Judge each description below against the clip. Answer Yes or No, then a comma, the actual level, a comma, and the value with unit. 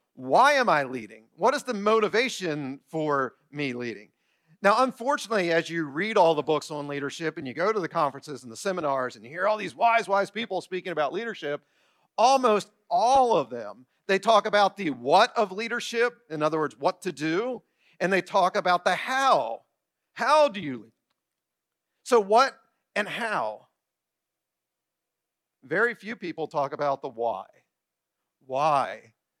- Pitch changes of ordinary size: No, wide, 7.4 semitones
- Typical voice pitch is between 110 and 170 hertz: No, medium, 185 Hz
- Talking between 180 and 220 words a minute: No, average, 165 wpm